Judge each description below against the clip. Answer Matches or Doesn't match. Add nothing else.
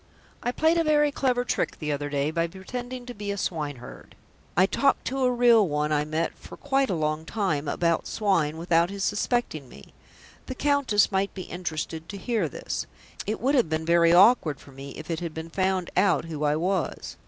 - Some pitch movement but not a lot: Doesn't match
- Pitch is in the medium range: Matches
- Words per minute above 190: Matches